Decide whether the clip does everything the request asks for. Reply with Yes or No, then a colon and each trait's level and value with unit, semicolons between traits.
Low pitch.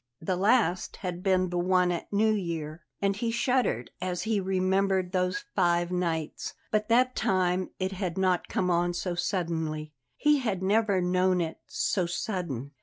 No: medium, 185 Hz